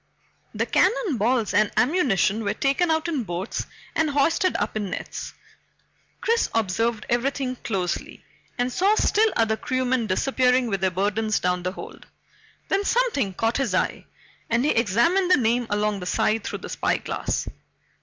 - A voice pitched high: Yes, high, 235 Hz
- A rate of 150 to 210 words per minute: Yes, average, 155 wpm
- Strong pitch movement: Yes, wide, 5.8 semitones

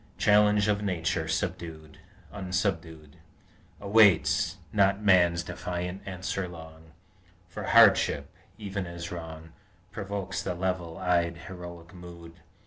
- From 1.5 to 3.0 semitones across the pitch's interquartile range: Yes, narrow, 2.6 semitones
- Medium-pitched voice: No, very low, 90 Hz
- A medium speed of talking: No, slow, 100 wpm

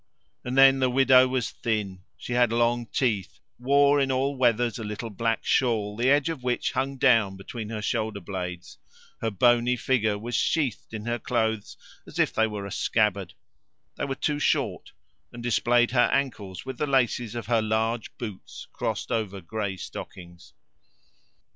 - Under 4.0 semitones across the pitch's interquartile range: Yes, average, 3.3 semitones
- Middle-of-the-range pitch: No, low, 115 Hz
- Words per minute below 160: No, average, 170 wpm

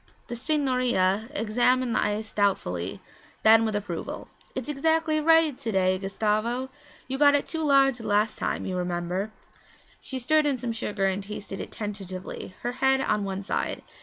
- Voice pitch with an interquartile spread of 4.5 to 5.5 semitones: Yes, average, 5.2 semitones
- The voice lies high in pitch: Yes, high, 225 Hz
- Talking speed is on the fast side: No, average, 165 wpm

